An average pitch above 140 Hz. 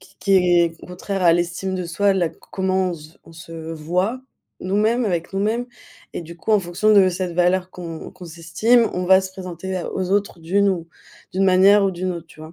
Yes: medium, 185 Hz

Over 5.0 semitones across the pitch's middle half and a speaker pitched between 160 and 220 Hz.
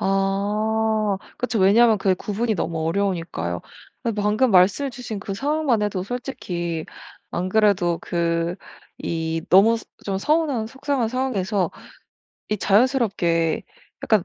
No: average, 4.1 semitones; high, 205 Hz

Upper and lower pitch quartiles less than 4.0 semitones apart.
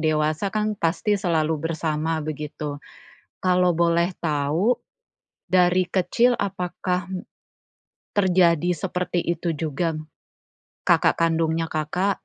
Yes: average, 2.8 semitones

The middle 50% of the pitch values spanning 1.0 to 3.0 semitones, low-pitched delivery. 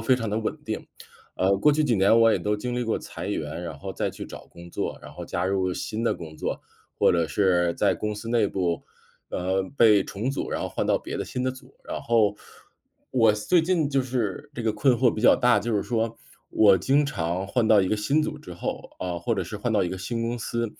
No: average, 4.3 semitones; low, 110 Hz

